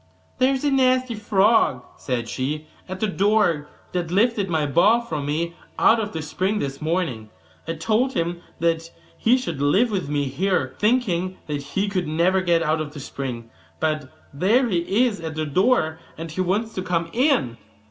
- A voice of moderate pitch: Yes, medium, 175 Hz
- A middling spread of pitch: No, wide, 5.7 semitones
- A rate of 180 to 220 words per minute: Yes, average, 185 wpm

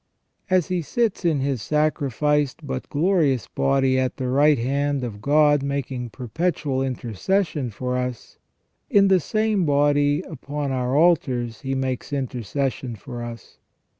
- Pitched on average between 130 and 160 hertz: Yes, medium, 140 Hz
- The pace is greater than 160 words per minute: No, slow, 135 wpm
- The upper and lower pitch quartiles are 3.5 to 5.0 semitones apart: No, average, 3.0 semitones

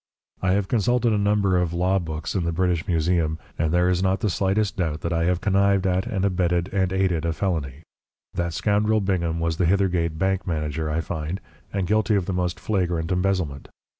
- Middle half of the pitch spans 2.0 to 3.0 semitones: Yes, average, 2.7 semitones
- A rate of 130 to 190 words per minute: No, average, 200 wpm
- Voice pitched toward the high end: No, very low, 90 Hz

